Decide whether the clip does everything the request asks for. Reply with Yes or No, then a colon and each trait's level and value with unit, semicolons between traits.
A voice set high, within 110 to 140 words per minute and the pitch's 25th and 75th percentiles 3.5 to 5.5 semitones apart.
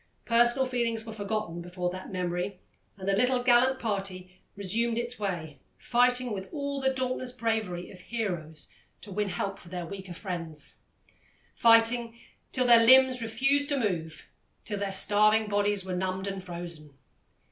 No: high, 205 Hz; average, 155 wpm; average, 4.6 semitones